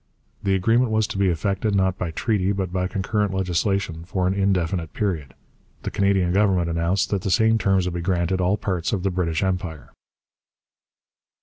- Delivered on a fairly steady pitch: Yes, narrow, 2.0 semitones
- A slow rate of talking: No, average, 180 wpm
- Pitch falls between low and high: No, very low, 95 Hz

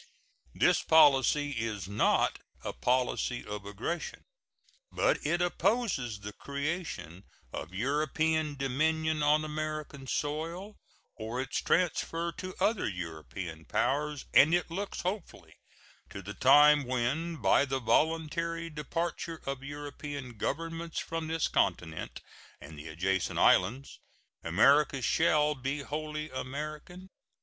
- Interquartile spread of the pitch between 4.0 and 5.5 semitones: Yes, average, 4.6 semitones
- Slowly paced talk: Yes, slow, 115 wpm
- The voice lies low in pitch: No, medium, 145 Hz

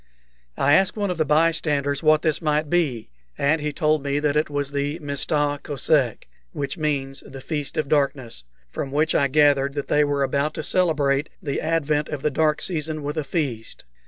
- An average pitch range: No, narrow, 1.7 semitones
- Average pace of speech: Yes, average, 190 wpm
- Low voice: No, medium, 145 Hz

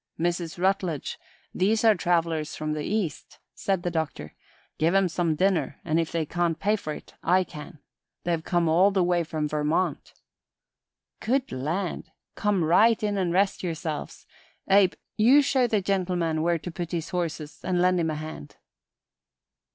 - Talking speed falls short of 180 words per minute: Yes, average, 165 wpm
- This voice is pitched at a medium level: Yes, medium, 175 Hz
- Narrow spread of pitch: No, average, 3.3 semitones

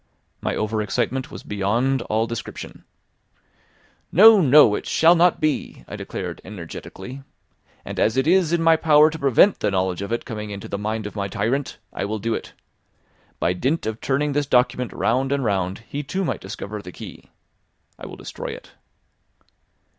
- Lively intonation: Yes, wide, 6.1 semitones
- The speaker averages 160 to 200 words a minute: Yes, average, 175 wpm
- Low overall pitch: Yes, low, 120 Hz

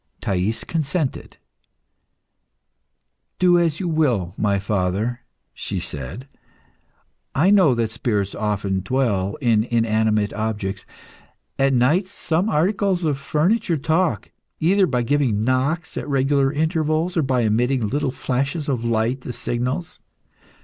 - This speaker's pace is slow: Yes, slow, 120 wpm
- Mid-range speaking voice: No, low, 130 Hz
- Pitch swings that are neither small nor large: No, wide, 6.3 semitones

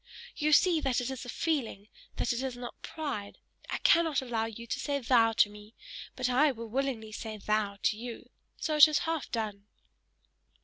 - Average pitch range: Yes, average, 4.5 semitones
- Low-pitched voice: No, high, 245 Hz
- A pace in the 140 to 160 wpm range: No, average, 190 wpm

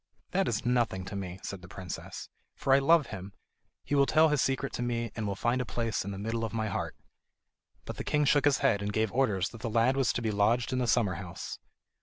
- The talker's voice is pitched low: Yes, low, 115 Hz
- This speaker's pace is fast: Yes, fast, 250 wpm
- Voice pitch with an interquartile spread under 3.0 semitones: No, average, 4.6 semitones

